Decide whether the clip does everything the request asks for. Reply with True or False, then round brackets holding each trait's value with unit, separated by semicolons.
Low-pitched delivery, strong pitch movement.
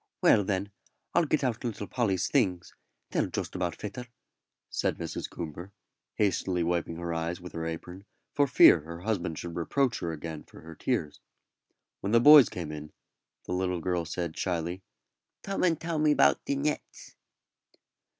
True (90 Hz; 6.2 semitones)